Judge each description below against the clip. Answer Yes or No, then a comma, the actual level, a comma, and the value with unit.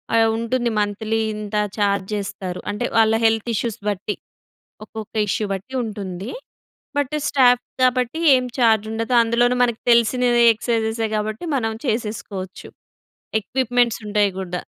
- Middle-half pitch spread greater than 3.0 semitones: No, average, 2.7 semitones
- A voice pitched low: No, high, 225 Hz